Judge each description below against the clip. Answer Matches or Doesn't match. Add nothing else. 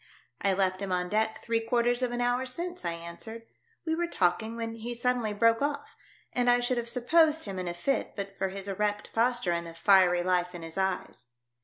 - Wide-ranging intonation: Doesn't match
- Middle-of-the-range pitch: Doesn't match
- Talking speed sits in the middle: Doesn't match